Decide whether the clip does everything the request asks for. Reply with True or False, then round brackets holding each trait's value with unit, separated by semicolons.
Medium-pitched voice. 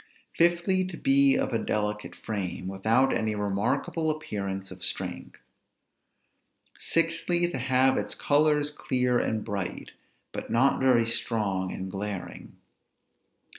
False (115 Hz)